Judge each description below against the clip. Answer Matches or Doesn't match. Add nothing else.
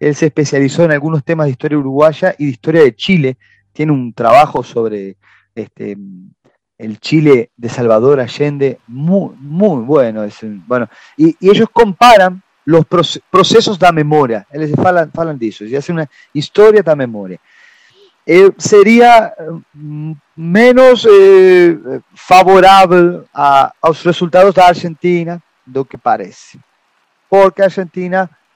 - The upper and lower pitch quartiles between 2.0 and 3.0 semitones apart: Doesn't match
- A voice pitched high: Doesn't match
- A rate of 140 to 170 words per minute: Doesn't match